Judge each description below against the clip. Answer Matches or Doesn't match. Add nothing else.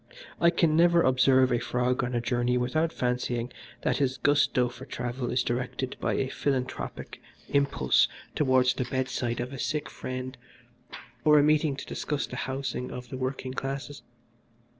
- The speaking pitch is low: Matches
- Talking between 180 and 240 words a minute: Doesn't match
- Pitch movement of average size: Doesn't match